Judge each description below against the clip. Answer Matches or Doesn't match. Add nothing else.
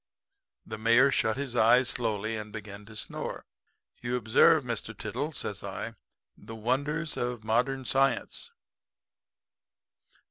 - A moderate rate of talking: Doesn't match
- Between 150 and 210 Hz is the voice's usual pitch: Doesn't match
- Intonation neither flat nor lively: Matches